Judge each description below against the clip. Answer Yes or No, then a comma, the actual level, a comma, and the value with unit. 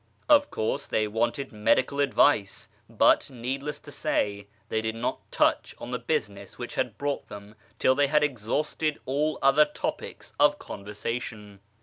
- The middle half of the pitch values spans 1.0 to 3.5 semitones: No, wide, 5.5 semitones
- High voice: No, low, 125 Hz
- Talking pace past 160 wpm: No, average, 150 wpm